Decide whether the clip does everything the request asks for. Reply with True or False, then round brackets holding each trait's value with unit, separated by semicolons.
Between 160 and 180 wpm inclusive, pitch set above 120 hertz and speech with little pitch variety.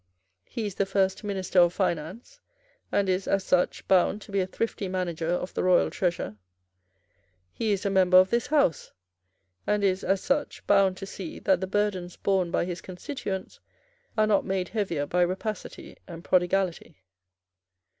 True (165 wpm; 190 Hz; 2.0 semitones)